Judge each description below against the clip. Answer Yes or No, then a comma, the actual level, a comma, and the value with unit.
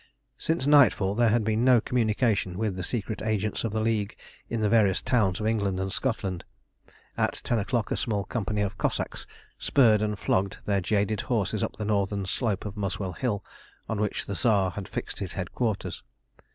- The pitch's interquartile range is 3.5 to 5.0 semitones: No, narrow, 2.4 semitones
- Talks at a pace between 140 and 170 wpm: No, average, 185 wpm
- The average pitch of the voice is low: Yes, low, 105 Hz